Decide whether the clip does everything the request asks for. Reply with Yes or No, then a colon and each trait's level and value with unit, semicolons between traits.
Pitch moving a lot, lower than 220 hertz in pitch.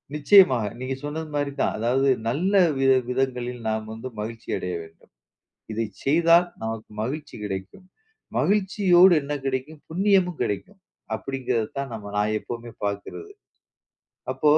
Yes: wide, 6.5 semitones; low, 135 Hz